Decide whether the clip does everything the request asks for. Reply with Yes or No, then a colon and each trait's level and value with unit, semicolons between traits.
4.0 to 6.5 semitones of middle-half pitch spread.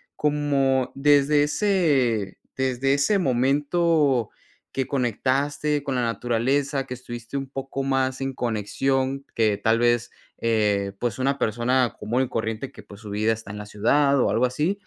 No: average, 3.3 semitones